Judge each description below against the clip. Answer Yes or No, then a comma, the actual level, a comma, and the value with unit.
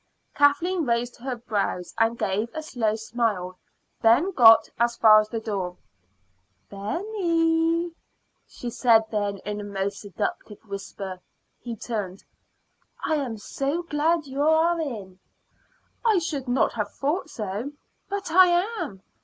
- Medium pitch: No, high, 235 Hz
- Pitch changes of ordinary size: No, wide, 7.4 semitones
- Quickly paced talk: No, slow, 135 wpm